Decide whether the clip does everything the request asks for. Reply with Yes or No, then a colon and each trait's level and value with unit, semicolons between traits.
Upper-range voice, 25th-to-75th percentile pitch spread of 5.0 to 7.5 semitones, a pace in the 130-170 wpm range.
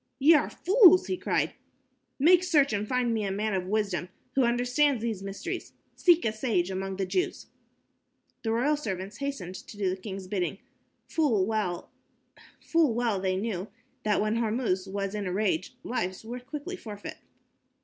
Yes: high, 215 Hz; wide, 5.5 semitones; average, 160 wpm